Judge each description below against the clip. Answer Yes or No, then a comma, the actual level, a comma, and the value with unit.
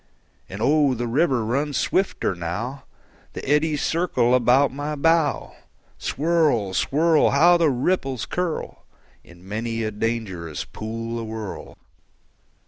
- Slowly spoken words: Yes, slow, 120 wpm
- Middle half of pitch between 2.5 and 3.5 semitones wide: No, average, 5.2 semitones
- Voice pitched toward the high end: No, low, 130 Hz